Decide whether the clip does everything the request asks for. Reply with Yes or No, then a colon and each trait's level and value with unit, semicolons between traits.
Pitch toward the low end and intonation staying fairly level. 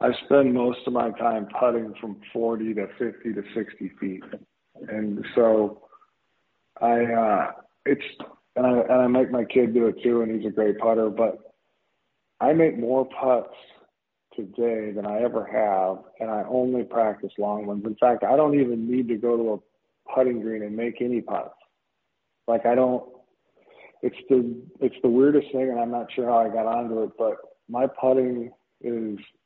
Yes: low, 115 Hz; narrow, 2.2 semitones